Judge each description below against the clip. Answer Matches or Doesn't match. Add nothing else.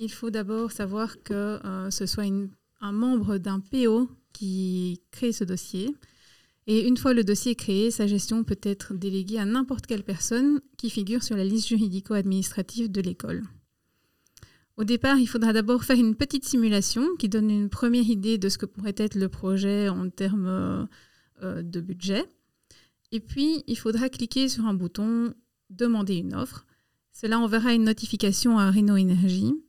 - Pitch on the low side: Doesn't match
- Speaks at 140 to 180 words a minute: Matches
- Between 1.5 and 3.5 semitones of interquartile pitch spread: Matches